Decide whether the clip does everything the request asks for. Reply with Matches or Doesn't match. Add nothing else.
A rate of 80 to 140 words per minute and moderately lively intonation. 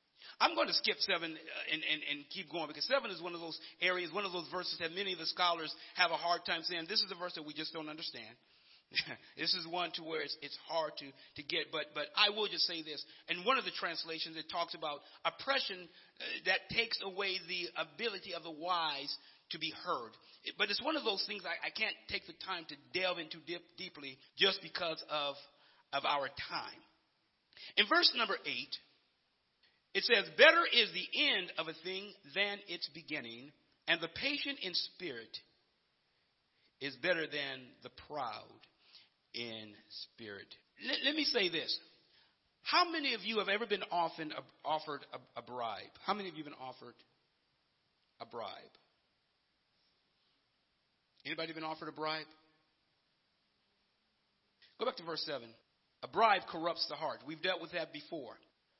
Doesn't match